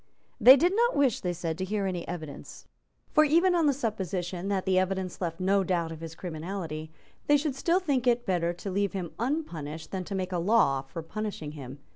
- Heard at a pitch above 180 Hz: Yes, high, 190 Hz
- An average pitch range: No, wide, 6.2 semitones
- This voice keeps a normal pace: No, fast, 210 wpm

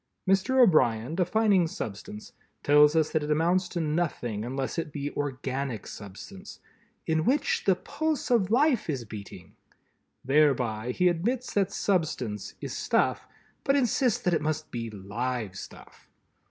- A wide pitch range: Yes, wide, 7.6 semitones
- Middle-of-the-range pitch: Yes, medium, 155 Hz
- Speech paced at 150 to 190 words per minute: No, average, 140 wpm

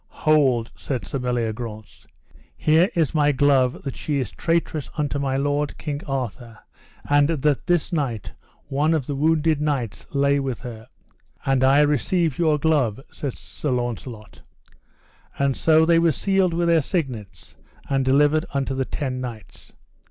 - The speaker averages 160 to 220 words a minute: No, average, 150 wpm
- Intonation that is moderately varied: Yes, average, 3.4 semitones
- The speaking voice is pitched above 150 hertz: No, medium, 140 Hz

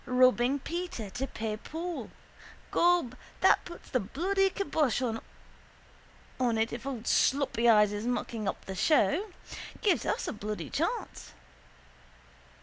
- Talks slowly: Yes, slow, 130 wpm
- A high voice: Yes, very high, 250 Hz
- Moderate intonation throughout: No, wide, 6.8 semitones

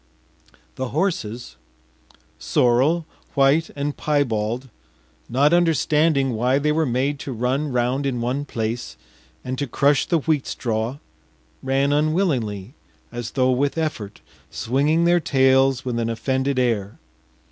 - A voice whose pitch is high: No, low, 135 Hz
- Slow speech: Yes, slow, 130 wpm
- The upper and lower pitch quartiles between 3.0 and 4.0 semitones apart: Yes, average, 3.4 semitones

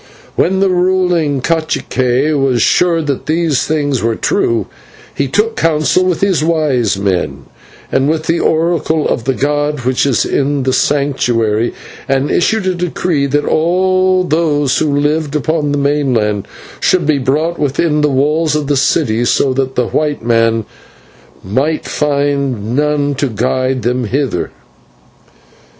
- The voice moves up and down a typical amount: Yes, average, 3.7 semitones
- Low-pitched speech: No, medium, 145 Hz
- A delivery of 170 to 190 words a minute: No, average, 145 wpm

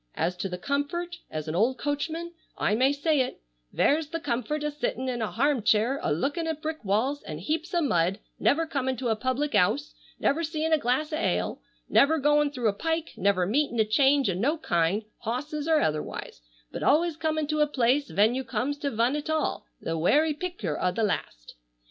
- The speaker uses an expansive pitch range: Yes, wide, 6.1 semitones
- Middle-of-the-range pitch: No, very high, 275 Hz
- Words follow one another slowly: No, fast, 205 wpm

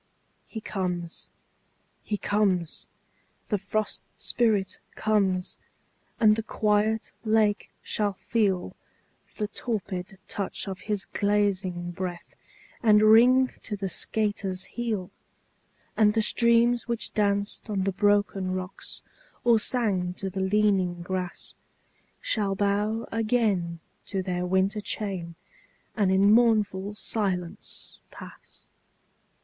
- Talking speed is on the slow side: Yes, slow, 110 wpm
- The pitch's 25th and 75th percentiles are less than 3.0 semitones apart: Yes, narrow, 2.5 semitones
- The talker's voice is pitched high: Yes, high, 205 Hz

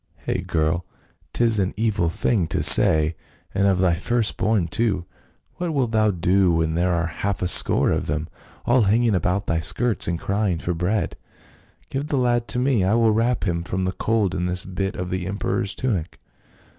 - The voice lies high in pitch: No, very low, 95 Hz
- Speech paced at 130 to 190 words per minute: No, average, 200 wpm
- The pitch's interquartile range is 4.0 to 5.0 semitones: Yes, average, 4.4 semitones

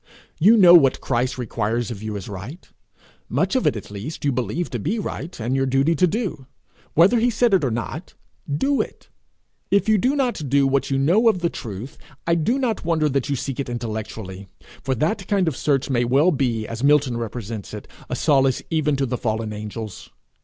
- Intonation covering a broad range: Yes, wide, 6.5 semitones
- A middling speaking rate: No, fast, 210 wpm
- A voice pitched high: No, low, 135 Hz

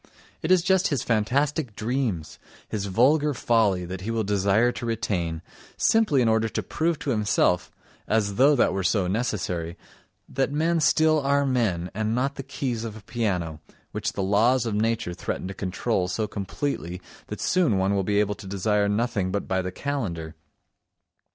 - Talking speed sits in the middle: Yes, average, 170 wpm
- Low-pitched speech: Yes, low, 110 Hz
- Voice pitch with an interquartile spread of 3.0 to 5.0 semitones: No, wide, 5.5 semitones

